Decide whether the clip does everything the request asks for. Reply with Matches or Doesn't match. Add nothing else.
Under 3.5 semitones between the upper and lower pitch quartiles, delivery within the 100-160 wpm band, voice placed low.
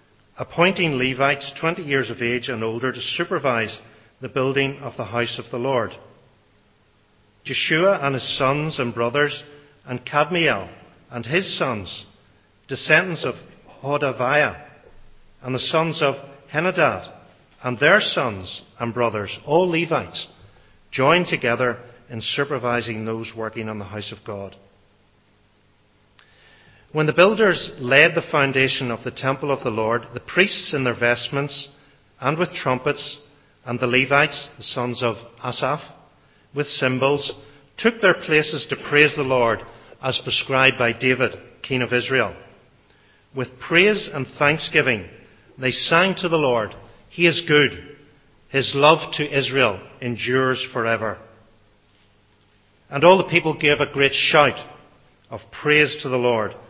Doesn't match